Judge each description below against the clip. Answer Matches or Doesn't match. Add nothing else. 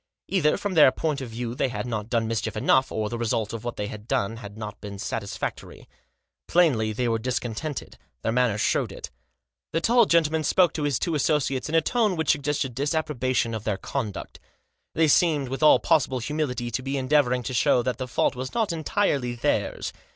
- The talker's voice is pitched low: Matches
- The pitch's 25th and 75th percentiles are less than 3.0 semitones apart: Doesn't match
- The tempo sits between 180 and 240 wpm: Matches